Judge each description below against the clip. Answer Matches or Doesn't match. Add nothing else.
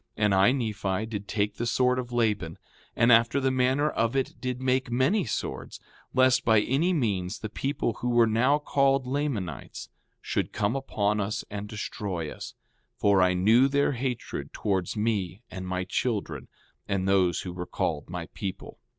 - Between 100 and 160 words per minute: Doesn't match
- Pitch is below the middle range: Matches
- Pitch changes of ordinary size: Matches